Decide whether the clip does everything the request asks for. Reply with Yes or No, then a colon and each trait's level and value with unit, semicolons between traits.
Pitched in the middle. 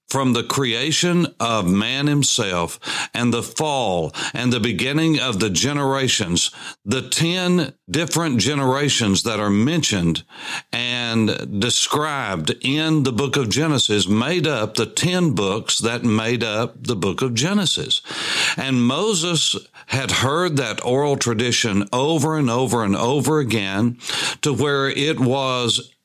No: low, 125 Hz